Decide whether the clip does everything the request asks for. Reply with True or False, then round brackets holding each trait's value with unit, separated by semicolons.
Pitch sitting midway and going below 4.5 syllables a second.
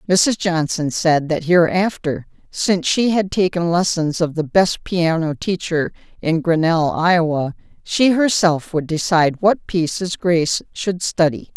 True (170 Hz; 4.3 syllables/s)